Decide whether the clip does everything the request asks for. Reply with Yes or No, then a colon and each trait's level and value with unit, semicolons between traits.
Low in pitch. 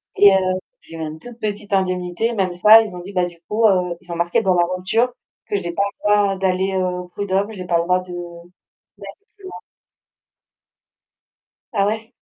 No: high, 190 Hz